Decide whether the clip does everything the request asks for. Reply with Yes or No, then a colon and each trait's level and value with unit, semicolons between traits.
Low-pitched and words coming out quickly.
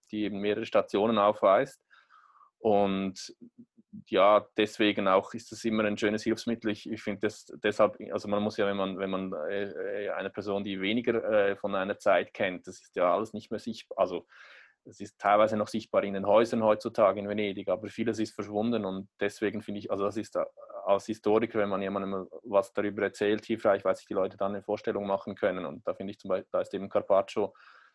Yes: low, 105 Hz; fast, 200 wpm